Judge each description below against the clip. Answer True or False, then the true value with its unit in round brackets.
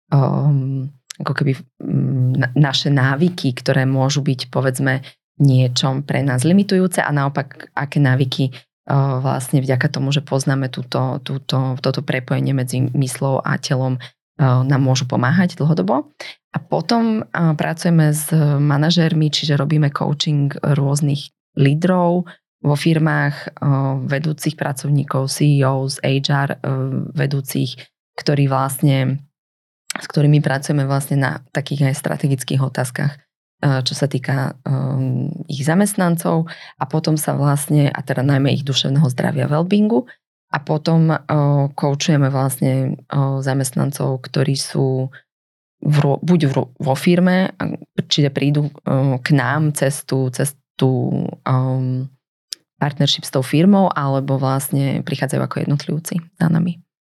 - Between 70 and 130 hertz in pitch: False (140 Hz)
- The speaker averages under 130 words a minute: True (110 wpm)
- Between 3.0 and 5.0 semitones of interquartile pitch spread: False (2.5 semitones)